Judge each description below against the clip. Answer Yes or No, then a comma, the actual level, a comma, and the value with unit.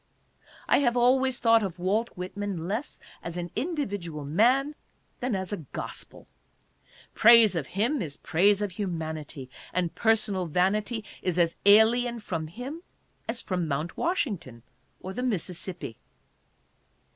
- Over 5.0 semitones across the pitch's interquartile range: Yes, wide, 5.5 semitones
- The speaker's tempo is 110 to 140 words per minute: Yes, slow, 135 wpm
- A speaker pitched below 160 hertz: No, high, 200 Hz